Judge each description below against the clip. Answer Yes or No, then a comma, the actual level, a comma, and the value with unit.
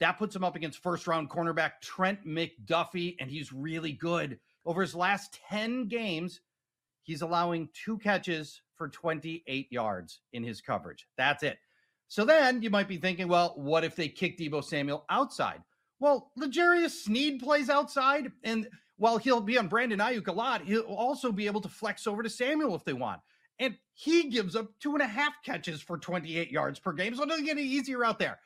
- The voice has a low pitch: No, high, 195 Hz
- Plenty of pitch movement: Yes, wide, 7.1 semitones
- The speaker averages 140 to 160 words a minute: No, average, 195 wpm